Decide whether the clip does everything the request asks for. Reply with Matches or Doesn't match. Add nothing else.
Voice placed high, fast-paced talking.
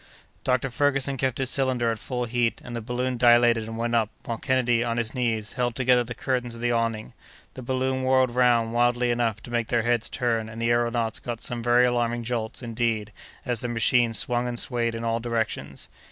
Doesn't match